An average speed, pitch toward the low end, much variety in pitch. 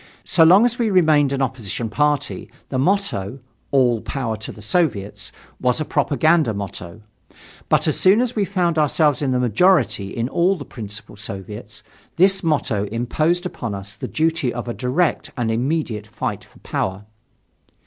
Yes: average, 165 wpm; low, 130 Hz; wide, 7.2 semitones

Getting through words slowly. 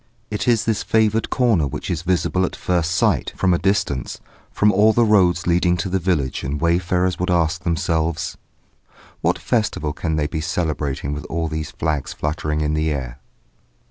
No: average, 175 wpm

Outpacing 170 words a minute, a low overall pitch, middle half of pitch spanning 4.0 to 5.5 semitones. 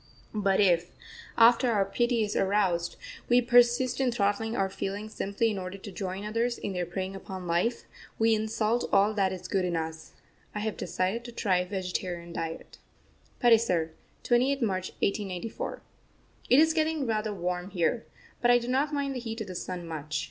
No: average, 180 wpm; high, 205 Hz; average, 4.3 semitones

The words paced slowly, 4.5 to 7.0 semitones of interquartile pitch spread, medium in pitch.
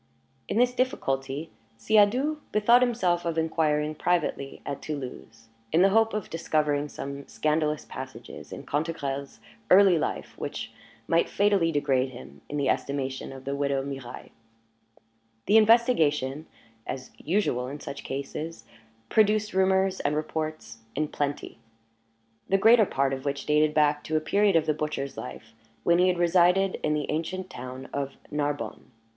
No: average, 150 wpm; average, 5.2 semitones; medium, 155 Hz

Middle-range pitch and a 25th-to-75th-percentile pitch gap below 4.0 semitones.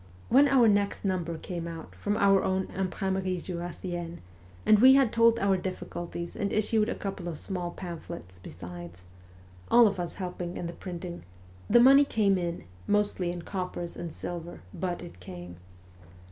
Yes: medium, 180 Hz; average, 2.9 semitones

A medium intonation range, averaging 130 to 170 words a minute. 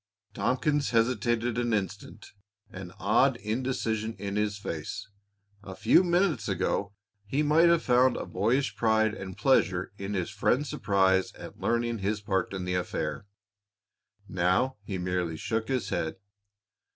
Yes: average, 4.6 semitones; average, 140 wpm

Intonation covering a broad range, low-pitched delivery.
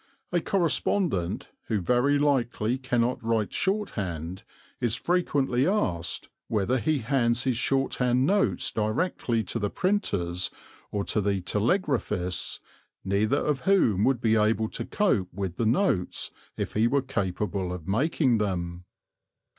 Yes: wide, 5.8 semitones; low, 115 Hz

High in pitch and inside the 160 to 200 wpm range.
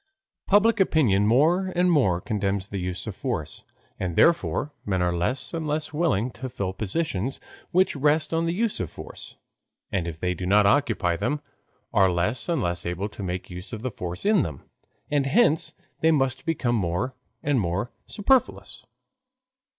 No: low, 120 Hz; average, 165 wpm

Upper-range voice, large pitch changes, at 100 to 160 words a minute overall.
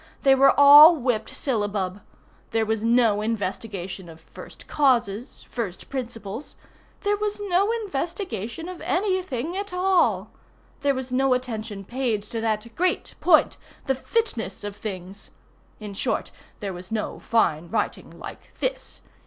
Yes: high, 235 Hz; wide, 6.7 semitones; average, 140 wpm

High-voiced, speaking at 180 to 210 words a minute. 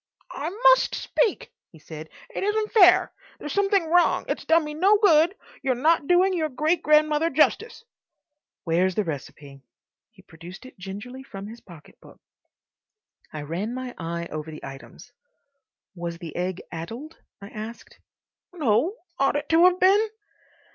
No: very high, 265 Hz; average, 155 wpm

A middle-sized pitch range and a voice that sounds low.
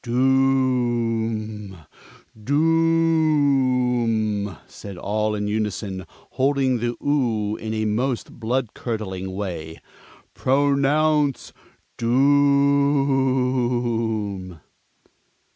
Yes: average, 4.3 semitones; low, 120 Hz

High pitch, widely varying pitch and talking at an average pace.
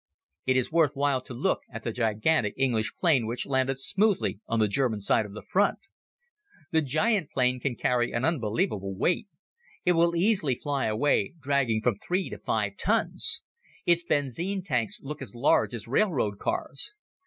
No: low, 135 Hz; wide, 6.1 semitones; average, 170 wpm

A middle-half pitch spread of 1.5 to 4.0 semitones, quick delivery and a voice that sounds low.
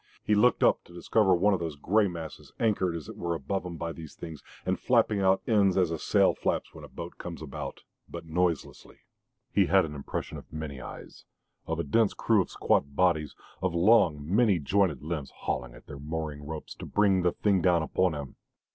Yes: average, 3.6 semitones; fast, 210 wpm; very low, 85 Hz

